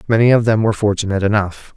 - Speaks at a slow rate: No, fast, 205 wpm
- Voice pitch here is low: Yes, low, 105 Hz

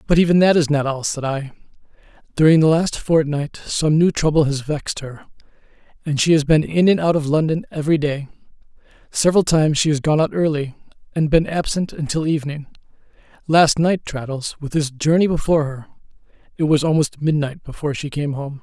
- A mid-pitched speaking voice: Yes, medium, 150 Hz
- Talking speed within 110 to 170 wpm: No, average, 185 wpm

